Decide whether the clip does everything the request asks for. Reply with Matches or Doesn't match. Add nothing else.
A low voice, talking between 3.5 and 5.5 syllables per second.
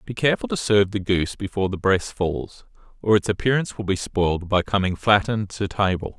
Doesn't match